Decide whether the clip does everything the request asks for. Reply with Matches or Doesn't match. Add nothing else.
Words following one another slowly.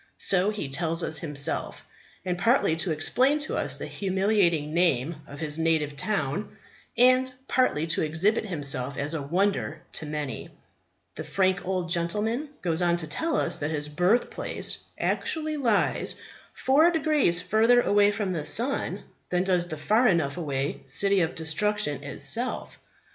Doesn't match